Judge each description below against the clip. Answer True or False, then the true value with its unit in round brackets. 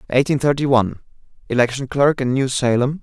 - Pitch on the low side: True (130 Hz)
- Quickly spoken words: False (140 wpm)